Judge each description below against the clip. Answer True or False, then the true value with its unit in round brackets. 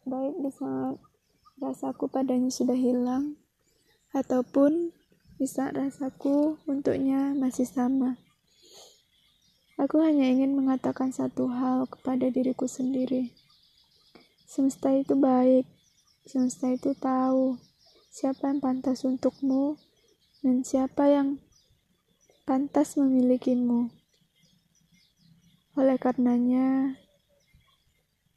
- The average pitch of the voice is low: False (260 Hz)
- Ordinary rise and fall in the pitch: False (1.5 semitones)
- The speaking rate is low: True (80 wpm)